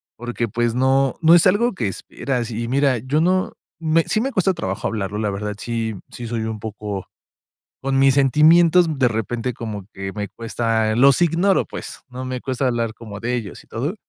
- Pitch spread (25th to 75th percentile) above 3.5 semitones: Yes, average, 4.6 semitones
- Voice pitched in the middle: No, low, 120 Hz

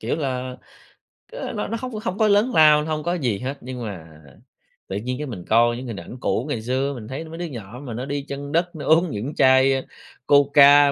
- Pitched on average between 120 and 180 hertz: Yes, medium, 140 Hz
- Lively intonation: No, average, 4.1 semitones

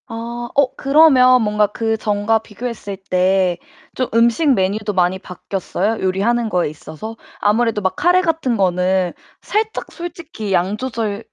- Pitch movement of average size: Yes, average, 4.6 semitones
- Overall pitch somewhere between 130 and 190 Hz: No, high, 220 Hz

